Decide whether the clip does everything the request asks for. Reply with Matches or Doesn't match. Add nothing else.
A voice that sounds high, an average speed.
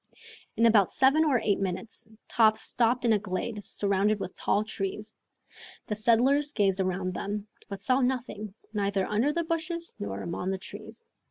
Matches